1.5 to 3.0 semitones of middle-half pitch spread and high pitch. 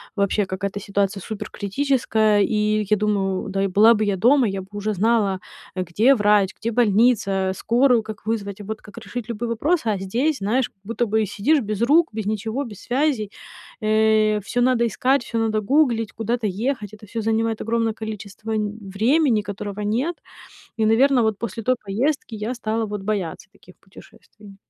Yes: narrow, 2.5 semitones; high, 215 Hz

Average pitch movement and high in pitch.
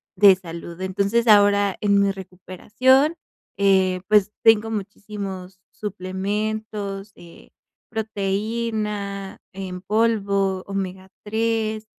No: narrow, 2.2 semitones; high, 200 Hz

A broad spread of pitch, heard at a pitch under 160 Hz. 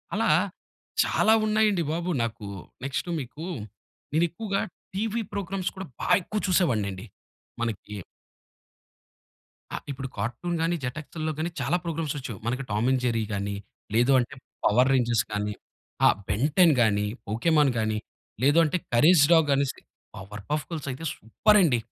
Yes: wide, 6.9 semitones; medium, 140 Hz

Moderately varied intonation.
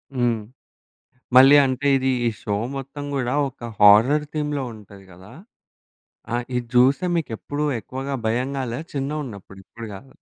Yes: average, 3.7 semitones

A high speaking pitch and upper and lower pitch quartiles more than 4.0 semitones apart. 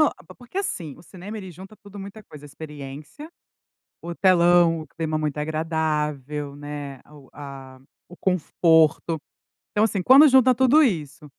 No: medium, 160 Hz; average, 4.9 semitones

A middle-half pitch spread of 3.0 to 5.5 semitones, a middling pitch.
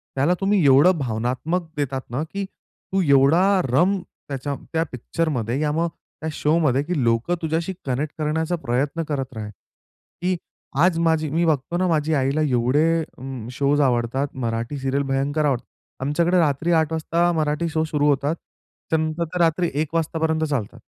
Yes: average, 3.6 semitones; medium, 150 Hz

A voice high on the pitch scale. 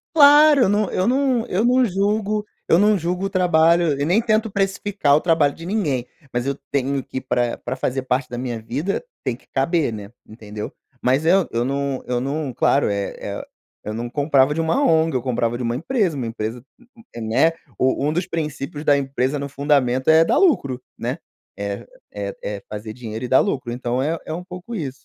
No: medium, 145 Hz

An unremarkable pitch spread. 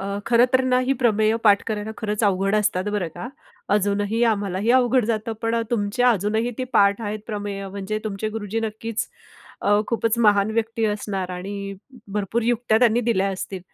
No: narrow, 2.2 semitones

